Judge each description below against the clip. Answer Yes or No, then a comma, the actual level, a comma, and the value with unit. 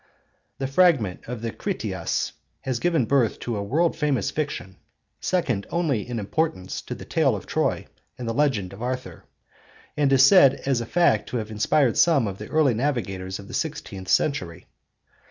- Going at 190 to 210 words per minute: No, average, 175 wpm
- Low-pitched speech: Yes, low, 125 Hz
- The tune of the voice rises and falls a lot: Yes, wide, 5.9 semitones